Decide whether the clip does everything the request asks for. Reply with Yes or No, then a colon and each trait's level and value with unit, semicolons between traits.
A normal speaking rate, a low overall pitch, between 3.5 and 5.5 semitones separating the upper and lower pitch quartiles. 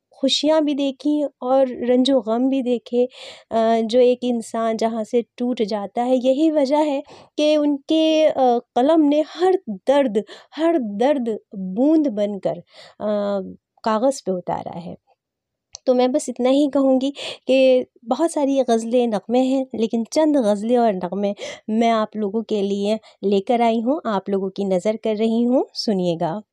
No: average, 150 wpm; high, 245 Hz; average, 4.0 semitones